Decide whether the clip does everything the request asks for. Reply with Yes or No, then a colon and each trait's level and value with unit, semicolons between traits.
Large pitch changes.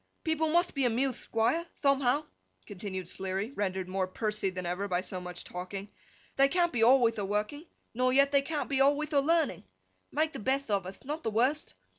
Yes: wide, 6.6 semitones